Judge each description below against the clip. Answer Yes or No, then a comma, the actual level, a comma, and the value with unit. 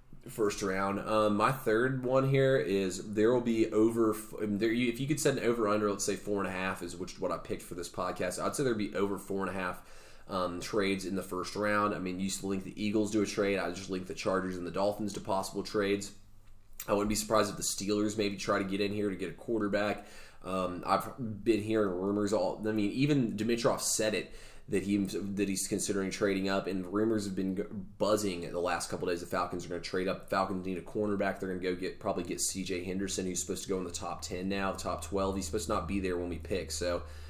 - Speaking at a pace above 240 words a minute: Yes, fast, 255 wpm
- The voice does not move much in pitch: Yes, narrow, 2.1 semitones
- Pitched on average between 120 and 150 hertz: No, low, 100 Hz